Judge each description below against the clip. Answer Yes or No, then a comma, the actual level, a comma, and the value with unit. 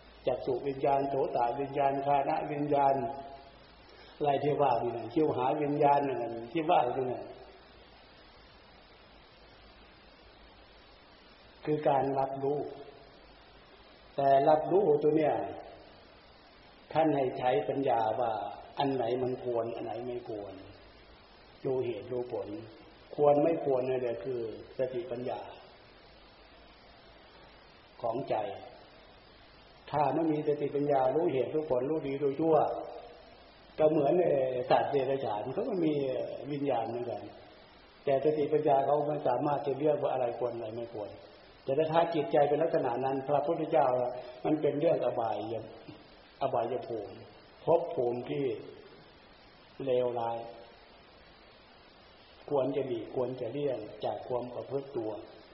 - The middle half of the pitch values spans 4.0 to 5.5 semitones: No, average, 3.3 semitones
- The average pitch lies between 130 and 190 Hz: Yes, low, 135 Hz